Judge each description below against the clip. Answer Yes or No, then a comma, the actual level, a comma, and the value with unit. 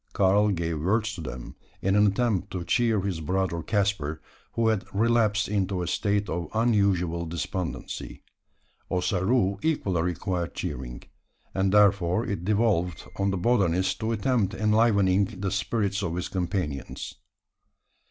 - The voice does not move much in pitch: No, average, 3.1 semitones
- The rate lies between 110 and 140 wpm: Yes, slow, 135 wpm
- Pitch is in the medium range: No, very low, 95 Hz